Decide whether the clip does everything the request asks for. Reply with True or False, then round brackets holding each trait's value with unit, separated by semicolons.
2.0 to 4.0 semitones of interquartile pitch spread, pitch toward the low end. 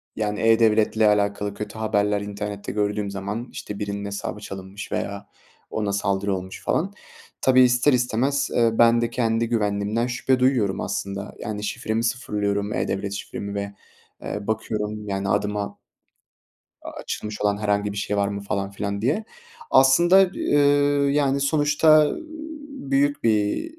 True (3.0 semitones; 105 Hz)